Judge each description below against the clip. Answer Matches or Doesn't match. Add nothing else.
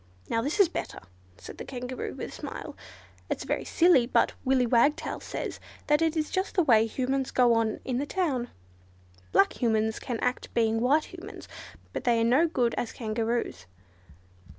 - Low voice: Doesn't match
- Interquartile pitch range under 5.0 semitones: Matches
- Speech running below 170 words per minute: Doesn't match